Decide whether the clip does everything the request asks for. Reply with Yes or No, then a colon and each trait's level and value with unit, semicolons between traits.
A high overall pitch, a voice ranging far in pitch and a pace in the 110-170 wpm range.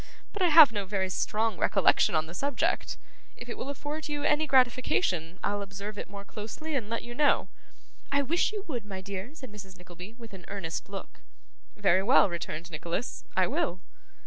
No: high, 210 Hz; wide, 6.7 semitones; average, 190 wpm